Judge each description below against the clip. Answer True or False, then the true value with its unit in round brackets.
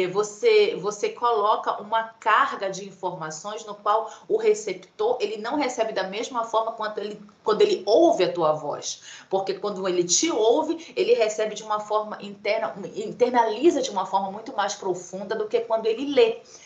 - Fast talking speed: False (170 wpm)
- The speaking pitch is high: True (220 Hz)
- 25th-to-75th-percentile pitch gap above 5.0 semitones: True (5.5 semitones)